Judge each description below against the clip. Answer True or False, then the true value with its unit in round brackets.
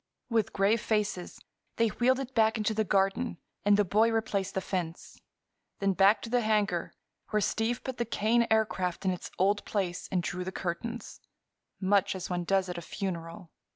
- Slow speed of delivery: False (180 wpm)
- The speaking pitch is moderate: False (200 Hz)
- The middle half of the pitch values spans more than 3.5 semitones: False (3.1 semitones)